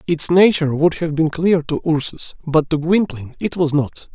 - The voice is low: No, medium, 160 Hz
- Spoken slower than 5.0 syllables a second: No, 5.1 syllables/s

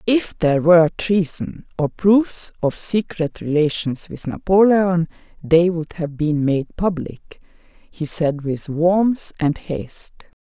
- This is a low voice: No, medium, 170 Hz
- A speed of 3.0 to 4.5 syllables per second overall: Yes, 3.6 syllables/s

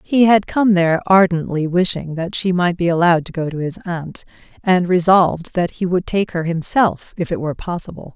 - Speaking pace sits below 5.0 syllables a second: No, 5.3 syllables/s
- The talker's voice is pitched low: No, medium, 175 Hz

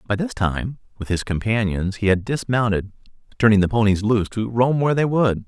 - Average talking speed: Yes, average, 195 wpm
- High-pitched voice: No, low, 110 Hz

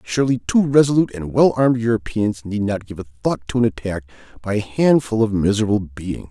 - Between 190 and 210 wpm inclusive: Yes, average, 200 wpm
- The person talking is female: No, male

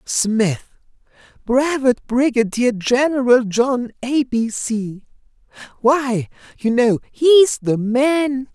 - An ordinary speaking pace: No, slow, 90 wpm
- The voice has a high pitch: Yes, high, 245 Hz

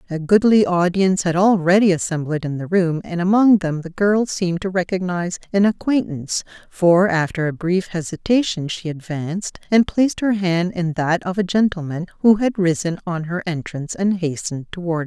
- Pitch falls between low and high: Yes, medium, 180 Hz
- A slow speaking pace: No, average, 180 wpm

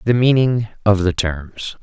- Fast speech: No, average, 165 wpm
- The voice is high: No, low, 105 Hz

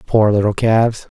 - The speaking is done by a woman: No, male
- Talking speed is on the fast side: No, average, 150 wpm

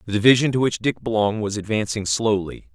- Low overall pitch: Yes, low, 110 Hz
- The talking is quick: No, average, 195 wpm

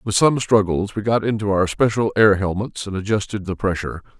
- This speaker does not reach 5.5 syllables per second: No, 5.6 syllables/s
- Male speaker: Yes, male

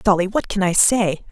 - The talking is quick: Yes, fast, 230 wpm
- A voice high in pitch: Yes, high, 195 Hz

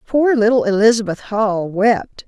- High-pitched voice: Yes, high, 215 Hz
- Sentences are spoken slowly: Yes, slow, 130 wpm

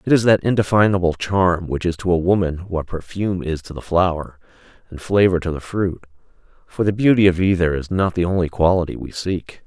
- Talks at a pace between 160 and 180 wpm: No, fast, 205 wpm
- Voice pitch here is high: No, very low, 90 Hz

